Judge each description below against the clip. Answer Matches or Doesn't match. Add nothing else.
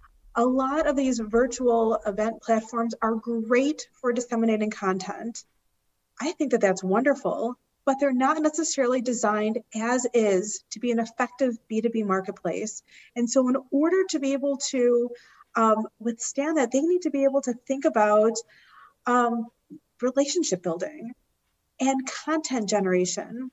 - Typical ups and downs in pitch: Matches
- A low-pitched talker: Doesn't match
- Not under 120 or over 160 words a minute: Matches